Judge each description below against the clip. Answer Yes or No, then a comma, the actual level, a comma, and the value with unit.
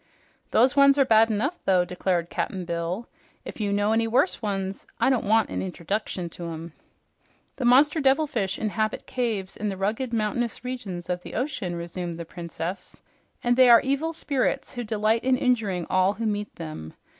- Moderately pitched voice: No, high, 215 Hz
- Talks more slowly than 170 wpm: No, average, 180 wpm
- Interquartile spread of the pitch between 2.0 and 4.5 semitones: No, average, 5.3 semitones